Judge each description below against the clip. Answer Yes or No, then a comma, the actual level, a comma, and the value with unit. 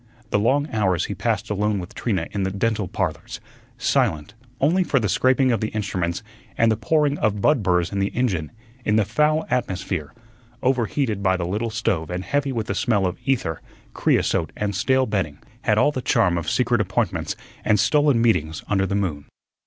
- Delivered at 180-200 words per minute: Yes, average, 190 wpm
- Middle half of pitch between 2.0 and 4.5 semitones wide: No, average, 5.0 semitones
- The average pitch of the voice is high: No, low, 105 Hz